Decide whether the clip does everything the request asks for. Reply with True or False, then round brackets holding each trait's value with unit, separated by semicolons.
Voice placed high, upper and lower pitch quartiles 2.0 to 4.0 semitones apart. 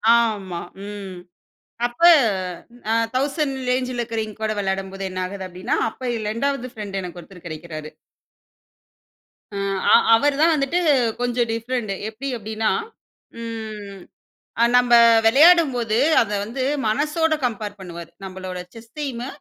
False (225 Hz; 4.5 semitones)